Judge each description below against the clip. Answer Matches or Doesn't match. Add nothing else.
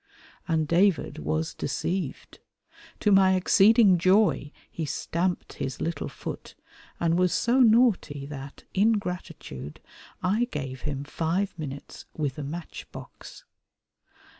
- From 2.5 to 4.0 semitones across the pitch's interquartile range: Doesn't match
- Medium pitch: Matches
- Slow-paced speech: Matches